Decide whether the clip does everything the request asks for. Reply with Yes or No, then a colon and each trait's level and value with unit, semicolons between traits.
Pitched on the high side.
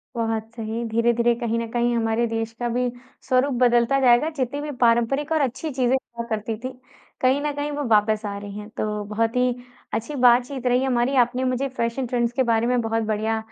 Yes: high, 235 Hz